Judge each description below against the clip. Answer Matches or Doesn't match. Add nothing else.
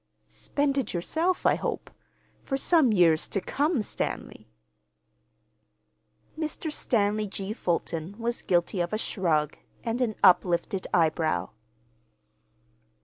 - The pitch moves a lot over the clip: Matches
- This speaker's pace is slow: Matches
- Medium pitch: Doesn't match